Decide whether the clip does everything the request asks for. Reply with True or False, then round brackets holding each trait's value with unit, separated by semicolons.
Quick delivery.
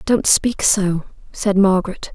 False (140 wpm)